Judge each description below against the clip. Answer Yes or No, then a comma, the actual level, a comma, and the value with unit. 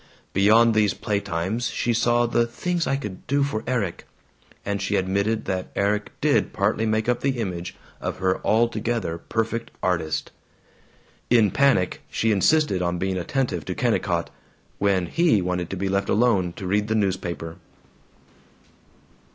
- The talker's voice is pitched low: Yes, low, 105 Hz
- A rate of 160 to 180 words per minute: No, average, 150 wpm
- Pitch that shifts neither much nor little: Yes, average, 4.1 semitones